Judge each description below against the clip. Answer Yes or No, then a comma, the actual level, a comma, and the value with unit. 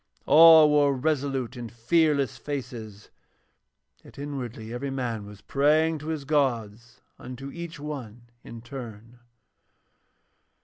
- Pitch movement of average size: Yes, average, 4.0 semitones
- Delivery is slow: Yes, slow, 115 wpm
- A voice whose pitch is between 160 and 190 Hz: No, low, 135 Hz